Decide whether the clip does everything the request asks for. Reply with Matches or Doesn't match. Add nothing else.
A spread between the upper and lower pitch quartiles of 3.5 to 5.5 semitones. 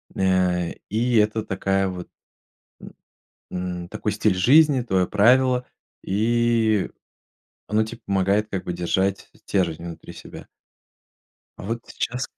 Matches